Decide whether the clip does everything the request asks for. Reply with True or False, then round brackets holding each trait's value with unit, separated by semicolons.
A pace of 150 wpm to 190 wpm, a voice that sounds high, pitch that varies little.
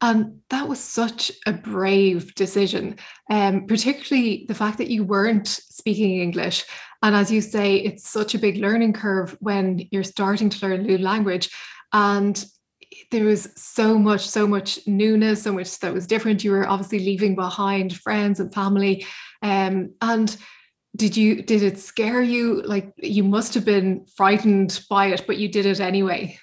True (175 wpm; 205 Hz; 1.7 semitones)